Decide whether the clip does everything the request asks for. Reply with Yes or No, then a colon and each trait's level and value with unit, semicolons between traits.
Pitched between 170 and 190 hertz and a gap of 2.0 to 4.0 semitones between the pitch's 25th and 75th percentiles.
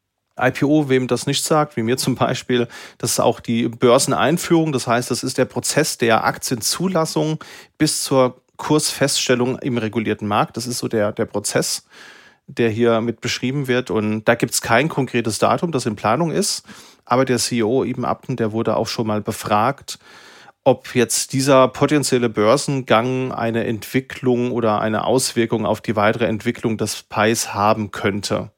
No: low, 120 Hz; average, 3.0 semitones